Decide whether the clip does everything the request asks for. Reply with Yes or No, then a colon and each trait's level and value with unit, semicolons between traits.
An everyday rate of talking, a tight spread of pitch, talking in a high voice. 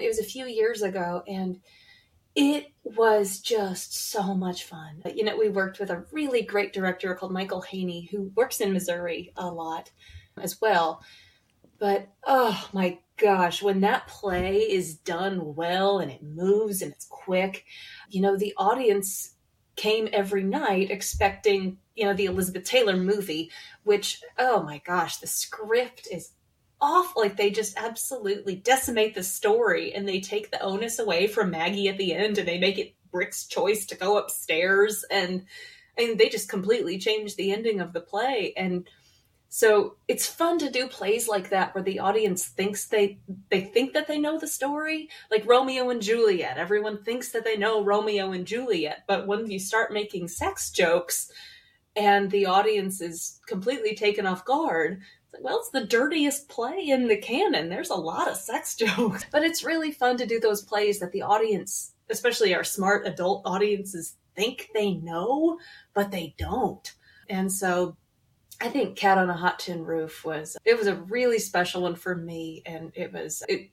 No: average, 175 wpm; average, 3.8 semitones; high, 205 Hz